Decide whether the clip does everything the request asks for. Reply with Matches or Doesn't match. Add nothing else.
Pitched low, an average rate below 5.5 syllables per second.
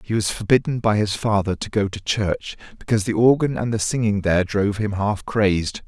Doesn't match